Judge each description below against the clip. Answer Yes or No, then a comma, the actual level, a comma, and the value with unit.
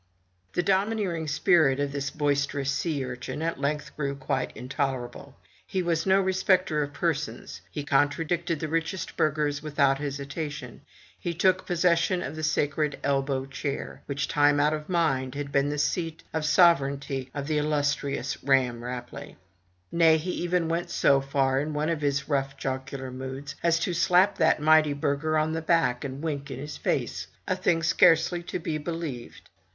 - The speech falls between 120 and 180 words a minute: Yes, average, 170 wpm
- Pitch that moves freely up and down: No, average, 3.0 semitones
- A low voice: No, medium, 150 Hz